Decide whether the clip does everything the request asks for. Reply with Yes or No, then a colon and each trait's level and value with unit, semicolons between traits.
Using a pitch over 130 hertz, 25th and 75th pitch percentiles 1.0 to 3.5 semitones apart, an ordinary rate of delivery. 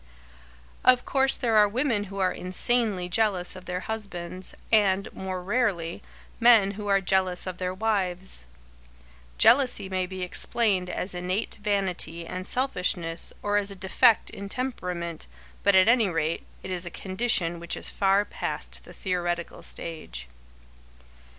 Yes: high, 190 Hz; average, 2.8 semitones; average, 145 wpm